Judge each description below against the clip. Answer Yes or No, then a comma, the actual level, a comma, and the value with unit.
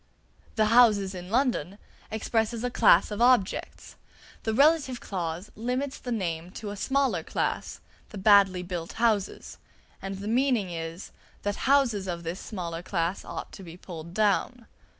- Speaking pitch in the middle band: No, high, 205 Hz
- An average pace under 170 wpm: Yes, average, 150 wpm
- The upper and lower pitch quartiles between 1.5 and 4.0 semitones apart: No, average, 4.9 semitones